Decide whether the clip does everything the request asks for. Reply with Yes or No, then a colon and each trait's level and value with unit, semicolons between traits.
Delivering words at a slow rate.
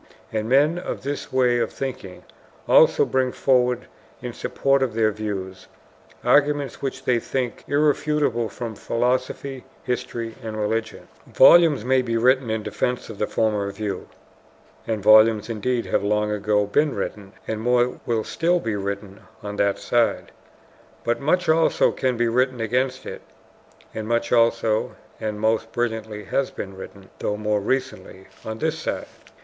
No: average, 155 wpm